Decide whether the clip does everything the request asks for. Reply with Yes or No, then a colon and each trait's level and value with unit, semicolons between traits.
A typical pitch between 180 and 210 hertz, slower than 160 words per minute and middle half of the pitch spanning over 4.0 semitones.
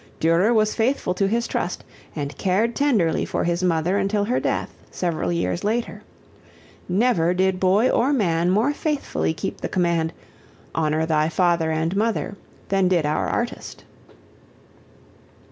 Yes: medium, 185 Hz; average, 145 wpm; average, 4.8 semitones